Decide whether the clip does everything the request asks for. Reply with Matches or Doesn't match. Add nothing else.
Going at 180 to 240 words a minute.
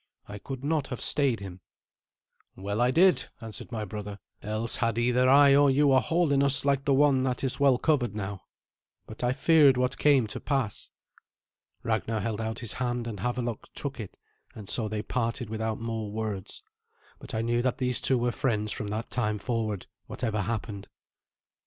Matches